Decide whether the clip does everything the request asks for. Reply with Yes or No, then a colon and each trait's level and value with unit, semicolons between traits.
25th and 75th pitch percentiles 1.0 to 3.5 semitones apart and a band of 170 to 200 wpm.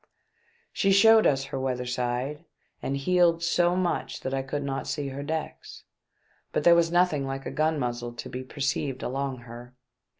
No: average, 4.3 semitones; average, 175 wpm